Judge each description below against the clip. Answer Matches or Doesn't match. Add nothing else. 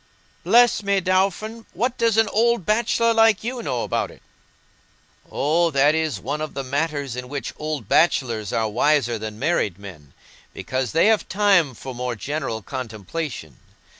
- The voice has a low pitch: Doesn't match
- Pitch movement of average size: Doesn't match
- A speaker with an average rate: Matches